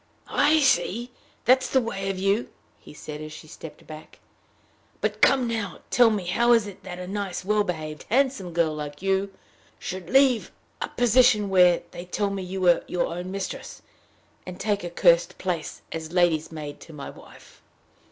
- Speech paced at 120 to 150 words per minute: No, average, 180 wpm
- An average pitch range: Yes, average, 4.4 semitones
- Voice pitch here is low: No, high, 190 Hz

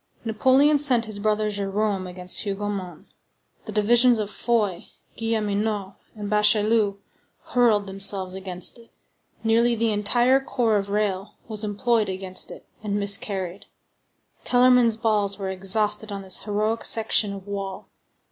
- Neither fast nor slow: No, slow, 130 wpm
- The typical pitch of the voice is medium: No, high, 210 Hz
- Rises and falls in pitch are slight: Yes, narrow, 2.3 semitones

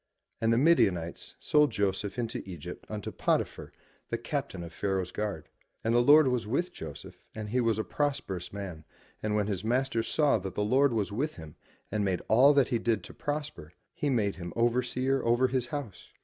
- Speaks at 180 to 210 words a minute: Yes, average, 195 wpm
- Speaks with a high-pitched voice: No, low, 115 Hz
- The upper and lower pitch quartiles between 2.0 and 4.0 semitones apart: No, average, 4.9 semitones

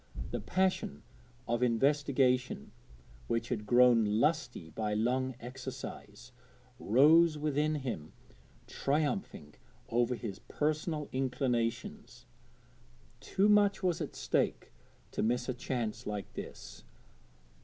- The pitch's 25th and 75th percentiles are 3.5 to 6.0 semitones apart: Yes, average, 4.4 semitones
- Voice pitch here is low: Yes, low, 125 Hz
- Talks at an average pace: No, slow, 100 wpm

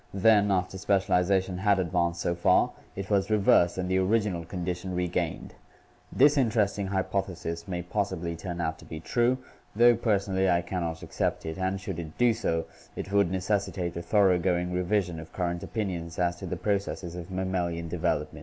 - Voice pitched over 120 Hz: No, very low, 95 Hz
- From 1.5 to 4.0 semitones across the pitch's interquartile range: Yes, narrow, 2.4 semitones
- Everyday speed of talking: Yes, average, 180 wpm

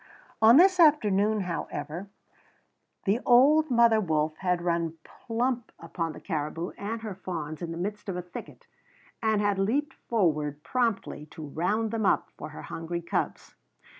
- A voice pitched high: Yes, high, 195 Hz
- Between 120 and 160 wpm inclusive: Yes, average, 155 wpm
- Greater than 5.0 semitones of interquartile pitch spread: Yes, wide, 5.4 semitones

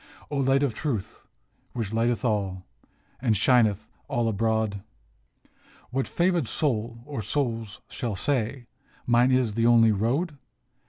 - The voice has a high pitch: No, low, 115 Hz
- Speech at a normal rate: No, slow, 130 wpm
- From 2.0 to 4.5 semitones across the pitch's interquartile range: Yes, average, 3.4 semitones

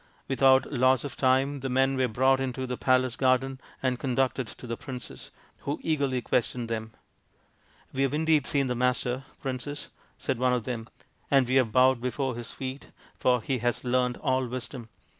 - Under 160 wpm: No, average, 185 wpm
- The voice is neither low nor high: No, low, 130 Hz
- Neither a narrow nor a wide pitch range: No, narrow, 1.3 semitones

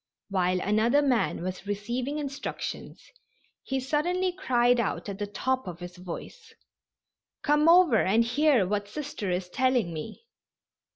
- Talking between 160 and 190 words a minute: No, slow, 135 wpm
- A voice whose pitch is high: Yes, high, 240 Hz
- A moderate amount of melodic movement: No, wide, 6.7 semitones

